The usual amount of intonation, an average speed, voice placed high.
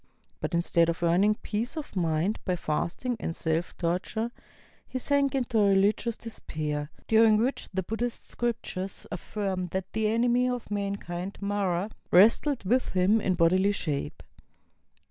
Yes: average, 4.5 semitones; average, 145 wpm; high, 200 Hz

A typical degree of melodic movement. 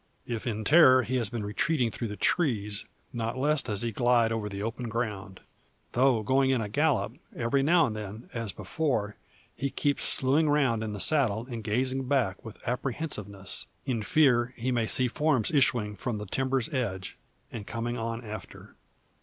Yes: average, 3.7 semitones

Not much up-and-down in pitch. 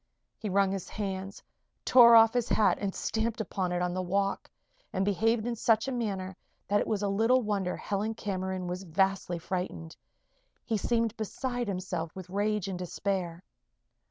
No: average, 3.1 semitones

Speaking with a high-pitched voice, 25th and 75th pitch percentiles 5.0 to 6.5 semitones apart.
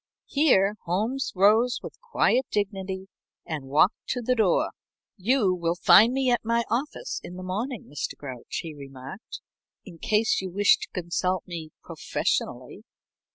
Yes: high, 195 Hz; wide, 5.4 semitones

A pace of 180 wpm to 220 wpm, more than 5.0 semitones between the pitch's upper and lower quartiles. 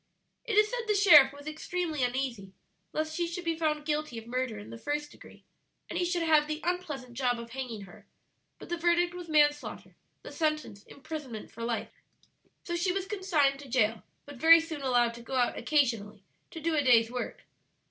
Yes: average, 200 wpm; wide, 5.4 semitones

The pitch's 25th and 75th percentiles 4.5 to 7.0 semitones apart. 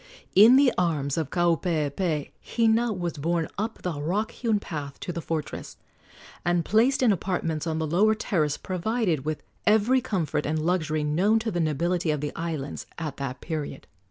Yes: average, 5.2 semitones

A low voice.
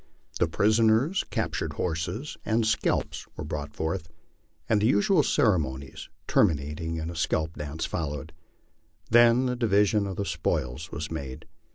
Yes: very low, 85 Hz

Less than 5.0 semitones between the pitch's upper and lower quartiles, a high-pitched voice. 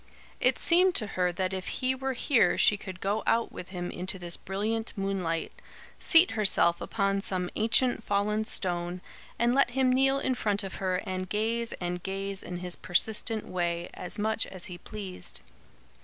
Yes: average, 3.9 semitones; high, 195 Hz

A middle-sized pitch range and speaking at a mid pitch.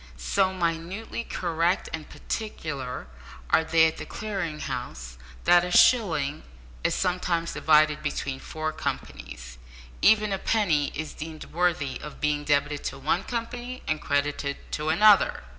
Yes: average, 4.0 semitones; medium, 160 Hz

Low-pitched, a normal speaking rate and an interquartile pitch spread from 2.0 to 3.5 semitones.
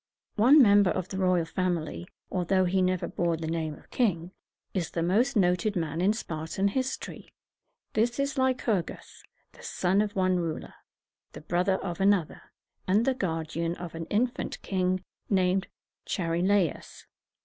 No: medium, 185 Hz; average, 160 wpm; average, 3.2 semitones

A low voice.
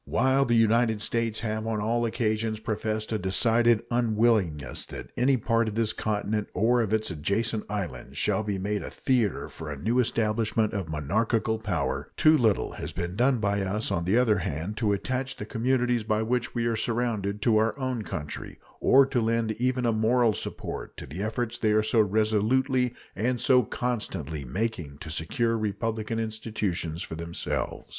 Yes: low, 110 Hz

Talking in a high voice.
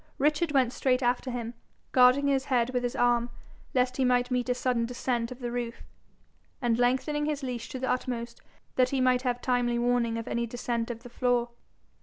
Yes: high, 245 Hz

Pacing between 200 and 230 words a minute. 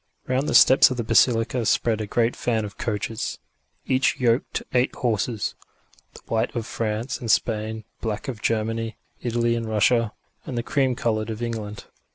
No: average, 180 wpm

